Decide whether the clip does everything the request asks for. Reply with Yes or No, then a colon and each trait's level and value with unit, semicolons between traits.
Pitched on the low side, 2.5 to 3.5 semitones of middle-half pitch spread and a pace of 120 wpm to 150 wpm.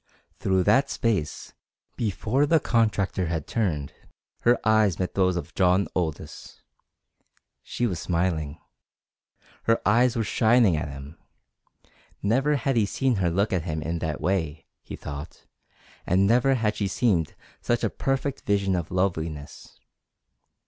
No: very low, 95 Hz; wide, 5.6 semitones; average, 140 wpm